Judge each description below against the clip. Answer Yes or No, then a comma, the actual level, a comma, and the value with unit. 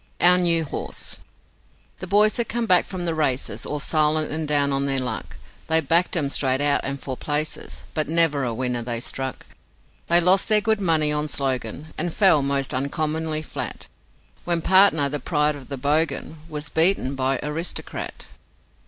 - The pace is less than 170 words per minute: No, average, 175 wpm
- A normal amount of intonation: Yes, average, 3.5 semitones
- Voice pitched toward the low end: No, medium, 150 Hz